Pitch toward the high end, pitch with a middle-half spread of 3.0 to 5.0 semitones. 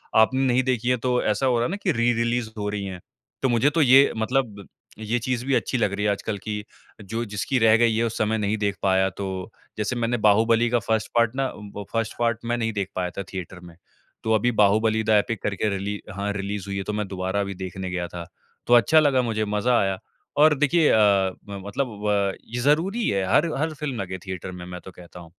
No: low, 110 Hz; average, 3.6 semitones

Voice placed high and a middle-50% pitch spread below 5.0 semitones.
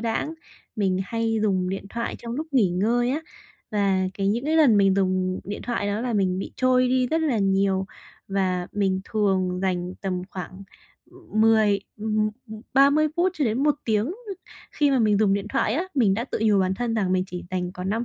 Yes: high, 210 Hz; average, 4.1 semitones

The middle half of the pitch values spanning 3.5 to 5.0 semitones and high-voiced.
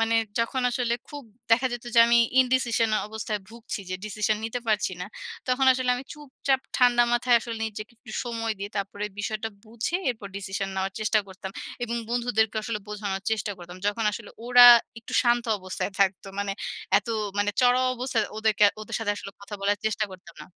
No: average, 2.8 semitones; high, 220 Hz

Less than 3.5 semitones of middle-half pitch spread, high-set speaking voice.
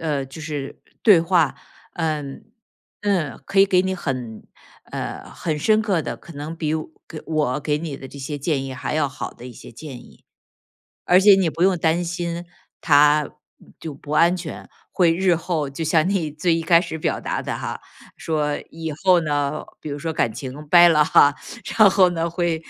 No: average, 3.0 semitones; medium, 160 Hz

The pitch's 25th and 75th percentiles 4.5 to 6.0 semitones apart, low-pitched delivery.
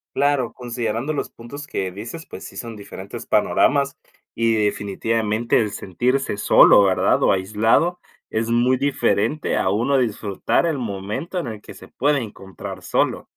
Yes: average, 5.0 semitones; low, 115 Hz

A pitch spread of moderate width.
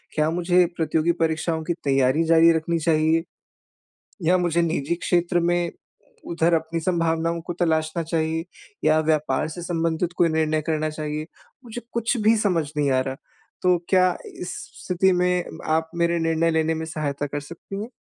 No: narrow, 1.8 semitones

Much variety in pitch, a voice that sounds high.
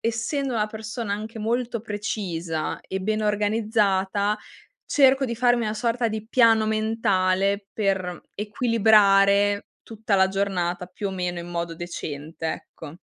No: average, 2.9 semitones; high, 210 Hz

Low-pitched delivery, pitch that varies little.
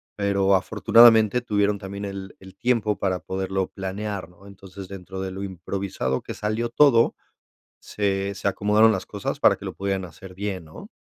Yes: low, 100 Hz; narrow, 1.6 semitones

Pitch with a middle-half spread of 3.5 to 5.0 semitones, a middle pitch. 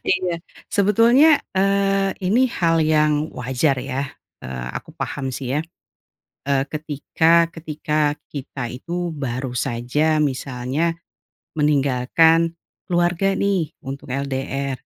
Yes: average, 4.1 semitones; medium, 150 Hz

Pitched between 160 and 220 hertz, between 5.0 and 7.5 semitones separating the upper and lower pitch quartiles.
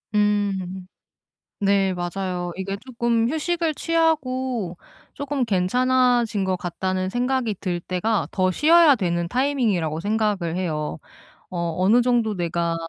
Yes: high, 205 Hz; wide, 5.6 semitones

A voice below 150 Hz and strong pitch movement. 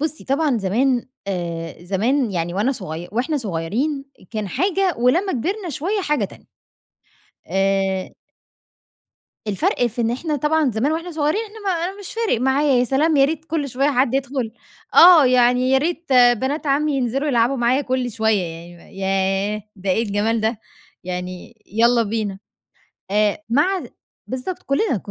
No: very high, 250 Hz; wide, 6.2 semitones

